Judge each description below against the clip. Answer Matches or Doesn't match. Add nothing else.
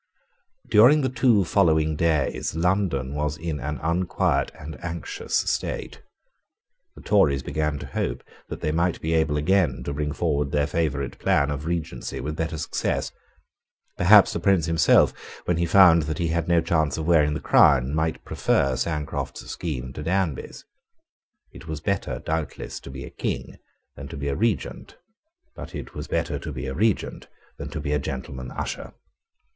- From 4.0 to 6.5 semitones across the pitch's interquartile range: Doesn't match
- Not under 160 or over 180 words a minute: Matches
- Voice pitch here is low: Matches